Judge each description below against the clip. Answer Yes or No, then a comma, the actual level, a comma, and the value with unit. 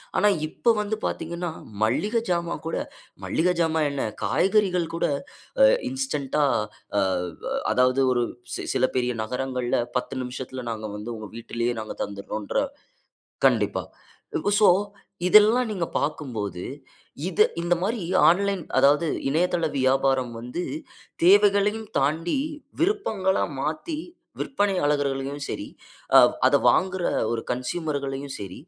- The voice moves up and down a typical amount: No, wide, 7.0 semitones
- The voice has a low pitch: No, medium, 155 Hz